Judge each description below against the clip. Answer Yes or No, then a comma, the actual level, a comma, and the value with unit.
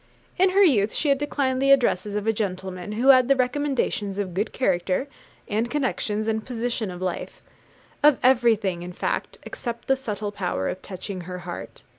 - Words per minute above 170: Yes, average, 180 wpm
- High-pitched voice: Yes, high, 220 Hz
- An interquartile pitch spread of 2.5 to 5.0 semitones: No, wide, 5.6 semitones